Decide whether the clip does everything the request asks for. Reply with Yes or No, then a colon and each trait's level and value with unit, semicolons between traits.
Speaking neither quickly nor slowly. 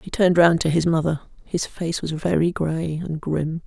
No: fast, 215 wpm